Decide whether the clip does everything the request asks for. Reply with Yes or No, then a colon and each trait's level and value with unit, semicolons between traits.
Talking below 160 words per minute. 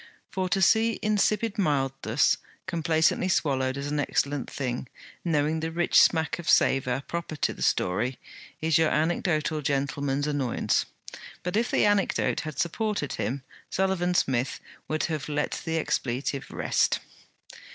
Yes: average, 140 wpm